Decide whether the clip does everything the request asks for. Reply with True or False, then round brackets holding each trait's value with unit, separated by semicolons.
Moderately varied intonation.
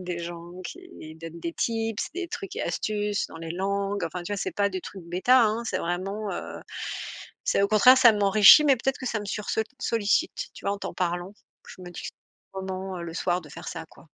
True (3.6 semitones)